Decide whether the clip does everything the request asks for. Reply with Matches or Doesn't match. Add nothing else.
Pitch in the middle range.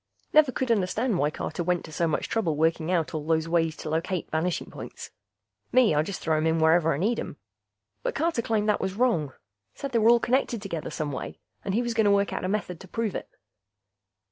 Matches